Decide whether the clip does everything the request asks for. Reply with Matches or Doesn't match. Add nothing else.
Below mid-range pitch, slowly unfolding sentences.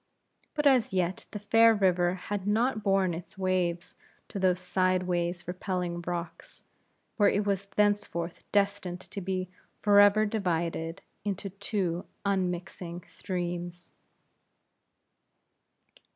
Doesn't match